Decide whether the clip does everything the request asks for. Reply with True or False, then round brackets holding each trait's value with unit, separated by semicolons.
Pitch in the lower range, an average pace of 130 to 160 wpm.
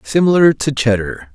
True (125 Hz; 135 wpm)